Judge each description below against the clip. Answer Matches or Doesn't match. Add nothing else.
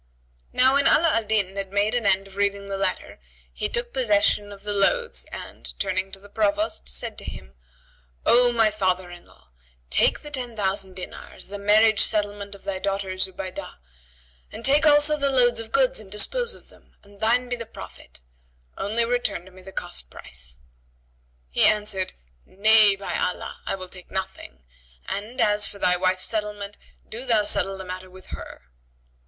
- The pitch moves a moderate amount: Matches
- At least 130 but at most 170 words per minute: Doesn't match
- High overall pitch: Matches